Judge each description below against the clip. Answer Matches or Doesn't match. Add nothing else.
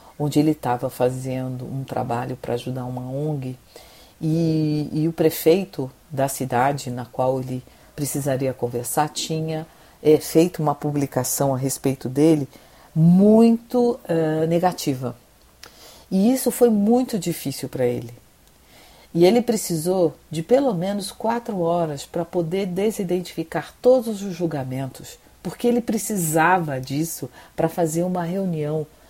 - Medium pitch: Matches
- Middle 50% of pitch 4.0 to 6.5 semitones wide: Matches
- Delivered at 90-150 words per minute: Matches